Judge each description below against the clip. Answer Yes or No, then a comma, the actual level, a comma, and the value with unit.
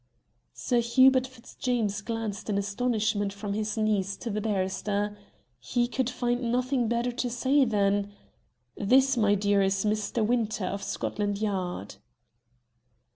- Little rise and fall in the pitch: No, average, 3.2 semitones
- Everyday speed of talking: No, slow, 130 wpm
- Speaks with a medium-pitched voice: No, high, 215 Hz